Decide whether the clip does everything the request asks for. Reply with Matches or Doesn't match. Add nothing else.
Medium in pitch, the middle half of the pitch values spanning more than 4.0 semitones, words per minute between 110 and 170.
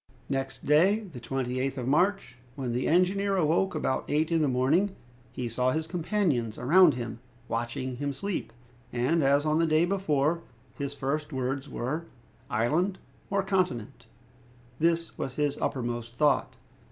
Matches